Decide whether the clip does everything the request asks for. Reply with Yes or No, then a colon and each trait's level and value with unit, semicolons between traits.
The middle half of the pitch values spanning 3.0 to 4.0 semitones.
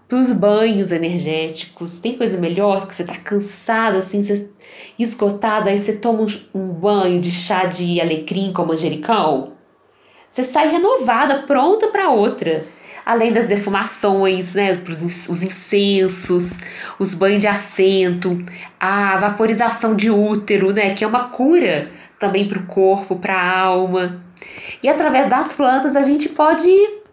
Yes: average, 3.7 semitones